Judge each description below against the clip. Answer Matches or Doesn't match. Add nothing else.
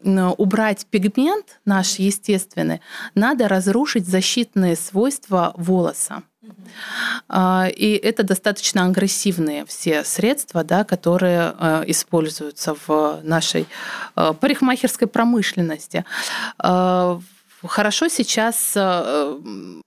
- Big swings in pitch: Doesn't match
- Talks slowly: Matches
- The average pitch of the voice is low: Doesn't match